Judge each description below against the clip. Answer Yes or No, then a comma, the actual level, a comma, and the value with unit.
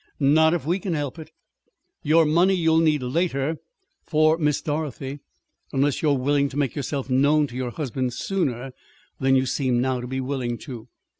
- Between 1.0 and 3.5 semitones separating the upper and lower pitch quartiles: Yes, average, 3.2 semitones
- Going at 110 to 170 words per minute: No, average, 180 wpm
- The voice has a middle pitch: Yes, medium, 145 Hz